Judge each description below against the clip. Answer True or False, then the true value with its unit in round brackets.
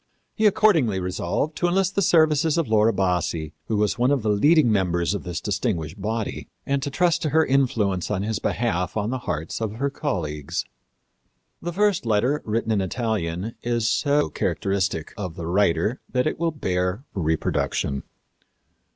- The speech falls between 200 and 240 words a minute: False (165 wpm)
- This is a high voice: False (110 Hz)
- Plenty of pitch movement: True (7.5 semitones)